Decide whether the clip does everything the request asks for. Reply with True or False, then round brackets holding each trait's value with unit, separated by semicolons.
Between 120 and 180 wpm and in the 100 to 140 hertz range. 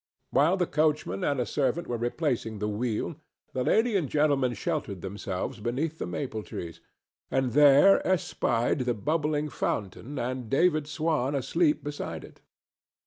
True (145 wpm; 135 Hz)